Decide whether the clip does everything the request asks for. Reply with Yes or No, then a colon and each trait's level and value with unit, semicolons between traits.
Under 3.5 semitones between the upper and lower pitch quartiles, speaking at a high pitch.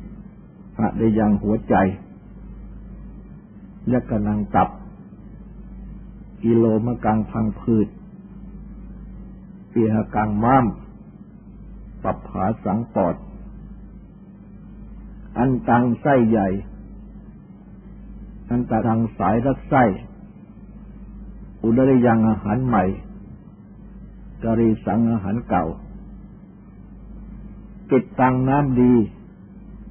No: average, 2.8 semitones; low, 115 Hz